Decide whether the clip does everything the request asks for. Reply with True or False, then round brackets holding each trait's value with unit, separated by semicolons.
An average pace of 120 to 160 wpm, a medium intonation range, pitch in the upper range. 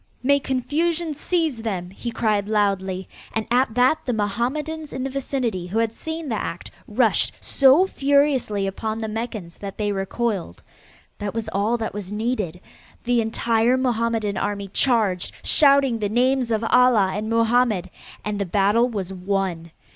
True (155 wpm; 4.0 semitones; 225 Hz)